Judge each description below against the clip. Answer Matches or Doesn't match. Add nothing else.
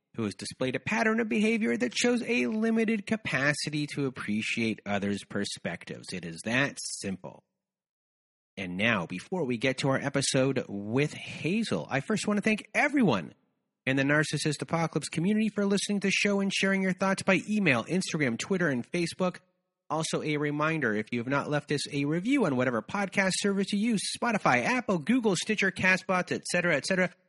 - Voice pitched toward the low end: Doesn't match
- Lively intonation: Matches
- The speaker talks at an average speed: Matches